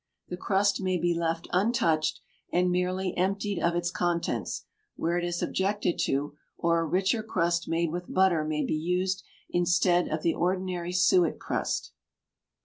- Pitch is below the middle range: No, medium, 175 Hz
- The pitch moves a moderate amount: No, narrow, 1.9 semitones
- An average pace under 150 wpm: No, average, 155 wpm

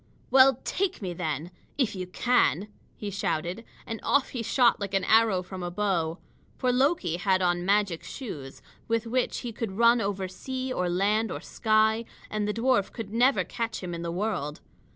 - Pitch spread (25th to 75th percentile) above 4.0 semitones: Yes, average, 4.4 semitones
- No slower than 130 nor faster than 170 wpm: No, average, 185 wpm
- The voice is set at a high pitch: Yes, high, 210 Hz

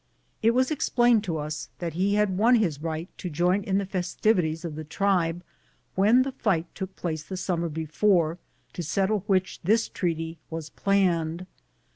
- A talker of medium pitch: Yes, medium, 180 Hz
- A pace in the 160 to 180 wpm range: Yes, average, 170 wpm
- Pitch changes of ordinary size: Yes, average, 3.7 semitones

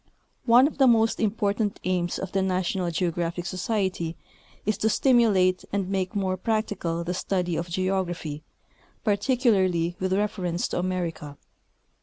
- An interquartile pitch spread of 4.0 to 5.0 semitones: No, average, 3.0 semitones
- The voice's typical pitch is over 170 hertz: Yes, medium, 185 Hz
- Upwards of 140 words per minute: No, slow, 135 wpm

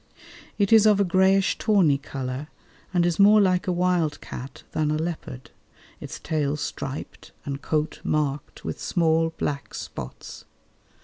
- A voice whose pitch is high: No, medium, 160 Hz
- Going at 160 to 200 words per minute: No, average, 145 wpm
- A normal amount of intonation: Yes, average, 4.6 semitones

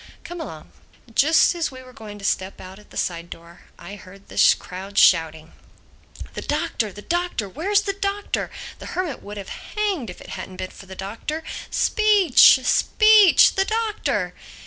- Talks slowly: No, average, 170 wpm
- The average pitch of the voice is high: Yes, high, 230 Hz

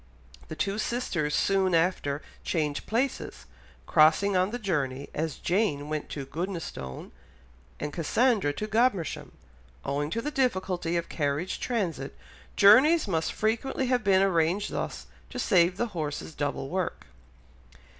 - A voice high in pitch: No, medium, 180 Hz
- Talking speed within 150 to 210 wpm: No, slow, 135 wpm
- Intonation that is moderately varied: No, wide, 5.8 semitones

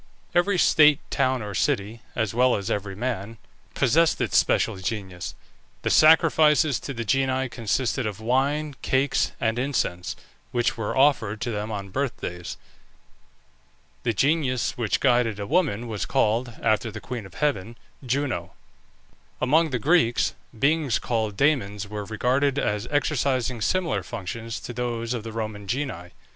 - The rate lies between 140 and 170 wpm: Yes, average, 145 wpm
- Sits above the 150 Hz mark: No, low, 120 Hz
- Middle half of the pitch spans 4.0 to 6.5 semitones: Yes, average, 4.6 semitones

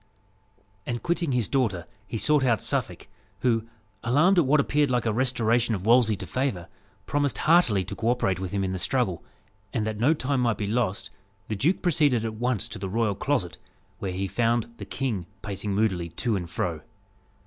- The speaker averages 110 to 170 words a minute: No, average, 190 wpm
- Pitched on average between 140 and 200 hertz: No, low, 115 Hz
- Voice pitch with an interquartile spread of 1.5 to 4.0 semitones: No, average, 4.6 semitones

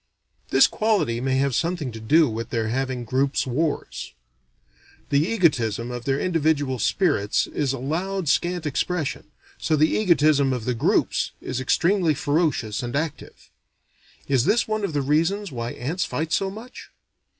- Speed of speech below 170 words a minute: Yes, average, 150 wpm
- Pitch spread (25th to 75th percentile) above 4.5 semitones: Yes, average, 5.1 semitones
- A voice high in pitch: No, medium, 145 Hz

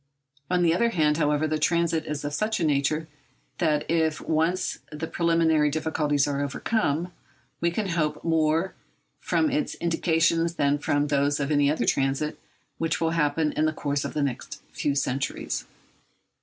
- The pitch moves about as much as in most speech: No, narrow, 2.3 semitones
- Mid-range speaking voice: Yes, medium, 155 Hz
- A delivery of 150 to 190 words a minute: Yes, average, 165 wpm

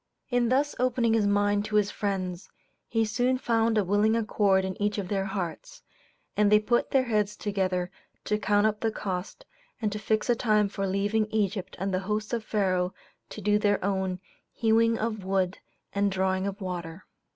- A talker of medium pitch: No, high, 205 Hz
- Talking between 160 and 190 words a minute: Yes, average, 185 wpm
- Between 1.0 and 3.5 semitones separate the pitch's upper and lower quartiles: Yes, narrow, 2.4 semitones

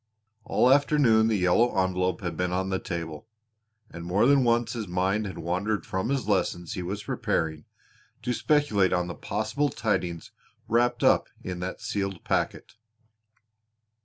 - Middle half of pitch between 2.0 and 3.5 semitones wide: No, average, 4.5 semitones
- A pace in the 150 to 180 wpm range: Yes, average, 160 wpm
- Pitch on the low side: Yes, very low, 95 Hz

